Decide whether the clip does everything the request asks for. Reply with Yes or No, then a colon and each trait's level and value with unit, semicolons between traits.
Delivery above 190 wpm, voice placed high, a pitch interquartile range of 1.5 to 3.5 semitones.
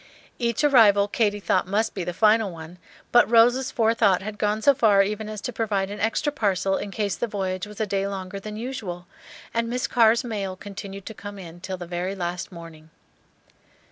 Yes: average, 200 wpm; high, 205 Hz; average, 3.0 semitones